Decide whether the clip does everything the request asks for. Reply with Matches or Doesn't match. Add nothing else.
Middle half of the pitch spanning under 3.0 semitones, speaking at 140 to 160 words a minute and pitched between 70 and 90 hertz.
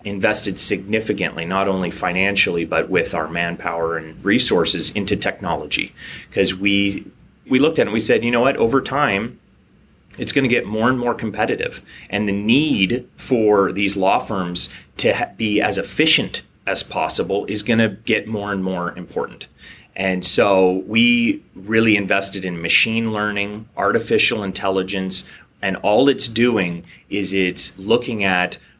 Doesn't match